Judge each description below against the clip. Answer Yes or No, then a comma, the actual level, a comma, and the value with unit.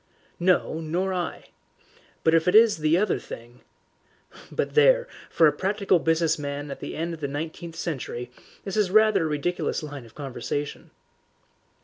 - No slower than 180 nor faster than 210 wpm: No, average, 160 wpm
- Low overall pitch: No, medium, 165 Hz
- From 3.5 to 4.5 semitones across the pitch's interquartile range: Yes, average, 4.2 semitones